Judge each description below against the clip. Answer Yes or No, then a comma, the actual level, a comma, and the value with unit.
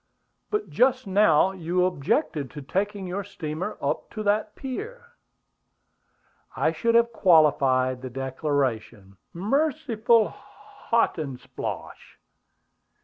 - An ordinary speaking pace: No, slow, 100 wpm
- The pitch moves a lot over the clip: Yes, wide, 8.3 semitones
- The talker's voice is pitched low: No, medium, 185 Hz